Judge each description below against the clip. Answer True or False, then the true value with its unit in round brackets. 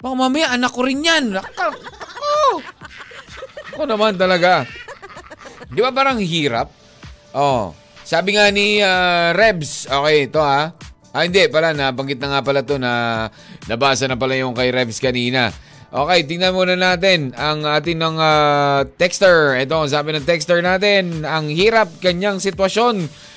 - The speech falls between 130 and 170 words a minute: True (150 wpm)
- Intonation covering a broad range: True (6.4 semitones)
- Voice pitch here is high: False (170 Hz)